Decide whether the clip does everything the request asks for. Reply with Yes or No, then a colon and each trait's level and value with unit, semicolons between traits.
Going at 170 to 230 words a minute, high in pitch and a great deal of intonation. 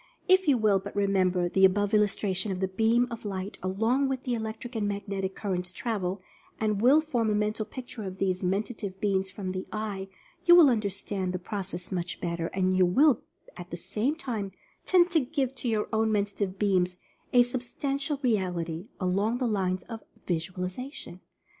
No: average, 185 wpm; high, 205 Hz; average, 4.1 semitones